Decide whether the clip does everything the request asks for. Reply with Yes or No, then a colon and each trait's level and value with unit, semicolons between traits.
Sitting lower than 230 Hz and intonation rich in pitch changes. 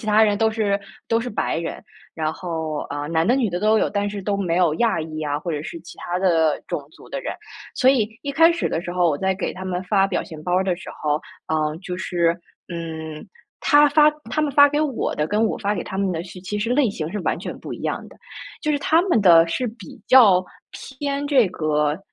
Yes: high, 190 Hz; wide, 5.8 semitones